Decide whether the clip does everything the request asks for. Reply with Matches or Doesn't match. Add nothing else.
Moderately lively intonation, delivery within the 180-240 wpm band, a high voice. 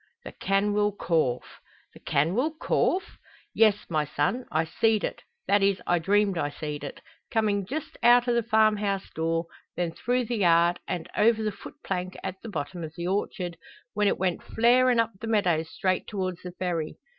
Matches